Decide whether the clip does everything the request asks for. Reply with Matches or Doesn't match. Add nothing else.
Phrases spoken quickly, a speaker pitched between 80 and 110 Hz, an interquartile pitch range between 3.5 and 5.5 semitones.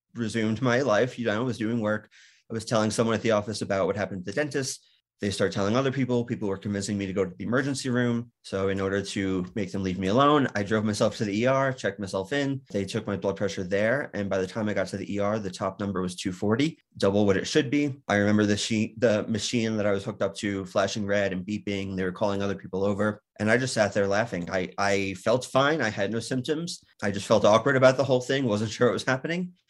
Matches